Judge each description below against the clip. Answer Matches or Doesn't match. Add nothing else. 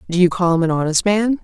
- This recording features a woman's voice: Matches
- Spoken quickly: Matches